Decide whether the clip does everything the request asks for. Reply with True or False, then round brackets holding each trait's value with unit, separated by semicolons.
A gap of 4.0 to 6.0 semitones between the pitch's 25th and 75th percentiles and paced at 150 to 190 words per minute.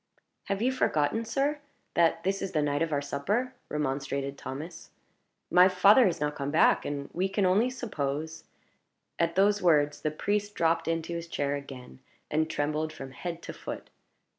True (5.1 semitones; 175 wpm)